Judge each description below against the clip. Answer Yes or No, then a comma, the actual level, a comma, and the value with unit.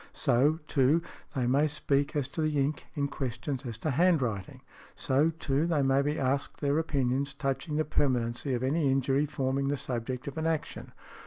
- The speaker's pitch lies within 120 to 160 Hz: Yes, medium, 140 Hz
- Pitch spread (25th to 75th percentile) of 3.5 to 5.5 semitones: No, narrow, 2.4 semitones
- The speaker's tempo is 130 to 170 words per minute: No, average, 180 wpm